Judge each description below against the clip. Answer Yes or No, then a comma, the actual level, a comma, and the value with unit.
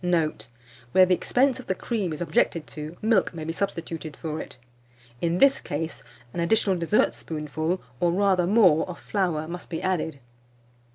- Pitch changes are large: No, average, 3.0 semitones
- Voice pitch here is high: No, medium, 170 Hz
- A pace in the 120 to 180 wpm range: Yes, average, 165 wpm